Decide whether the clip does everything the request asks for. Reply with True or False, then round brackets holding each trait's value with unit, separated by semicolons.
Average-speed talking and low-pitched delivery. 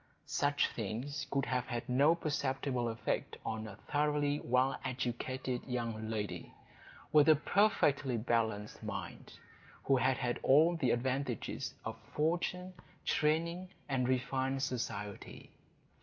False (120 wpm; 130 Hz)